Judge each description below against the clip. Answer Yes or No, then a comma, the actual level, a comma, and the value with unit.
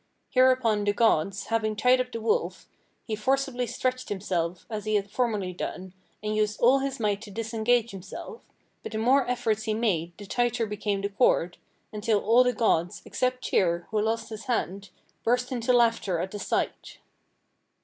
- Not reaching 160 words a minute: No, average, 175 wpm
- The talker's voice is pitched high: Yes, high, 220 Hz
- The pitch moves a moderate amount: Yes, average, 3.3 semitones